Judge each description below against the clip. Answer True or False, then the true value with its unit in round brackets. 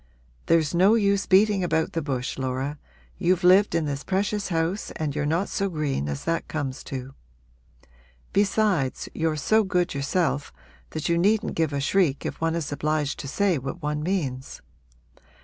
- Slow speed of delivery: False (165 wpm)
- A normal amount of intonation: True (5.0 semitones)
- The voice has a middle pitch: True (165 Hz)